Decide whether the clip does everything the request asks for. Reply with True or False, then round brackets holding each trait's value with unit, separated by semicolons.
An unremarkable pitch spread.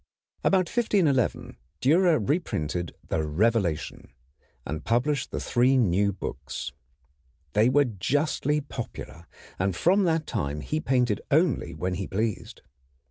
False (8.5 semitones)